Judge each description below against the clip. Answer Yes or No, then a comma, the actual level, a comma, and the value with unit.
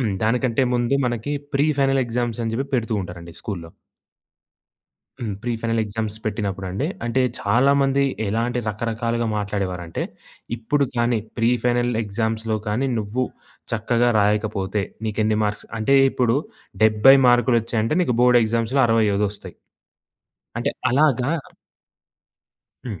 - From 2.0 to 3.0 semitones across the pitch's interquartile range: Yes, narrow, 2.6 semitones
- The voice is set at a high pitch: No, low, 115 Hz